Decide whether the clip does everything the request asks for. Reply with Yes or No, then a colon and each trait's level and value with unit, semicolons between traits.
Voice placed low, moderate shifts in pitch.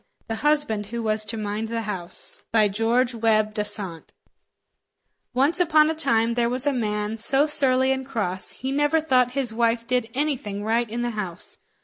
No: high, 230 Hz; average, 3.7 semitones